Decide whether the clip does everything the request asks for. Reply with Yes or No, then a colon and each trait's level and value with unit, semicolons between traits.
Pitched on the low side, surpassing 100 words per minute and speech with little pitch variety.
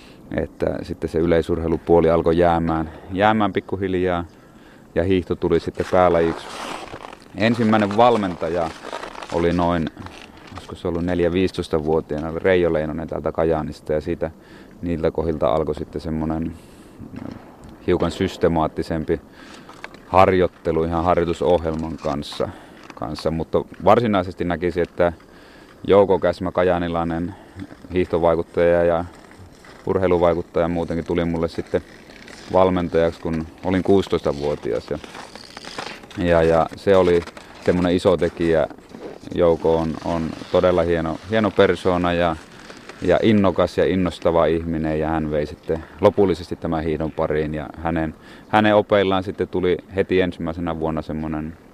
Yes: very low, 85 Hz; average, 110 wpm; narrow, 2.0 semitones